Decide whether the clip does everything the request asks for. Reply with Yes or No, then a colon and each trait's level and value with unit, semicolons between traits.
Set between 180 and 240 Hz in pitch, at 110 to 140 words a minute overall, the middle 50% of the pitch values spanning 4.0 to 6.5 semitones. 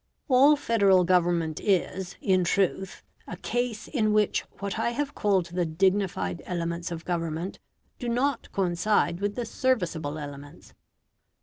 Yes: high, 190 Hz; slow, 135 wpm; average, 4.3 semitones